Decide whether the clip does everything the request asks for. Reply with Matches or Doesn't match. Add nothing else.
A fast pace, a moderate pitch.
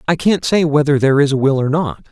Matches